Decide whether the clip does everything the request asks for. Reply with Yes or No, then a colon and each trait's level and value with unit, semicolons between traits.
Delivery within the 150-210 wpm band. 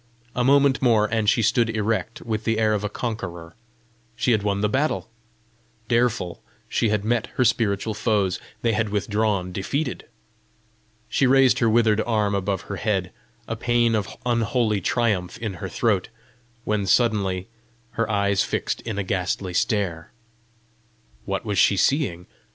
Yes: average, 155 wpm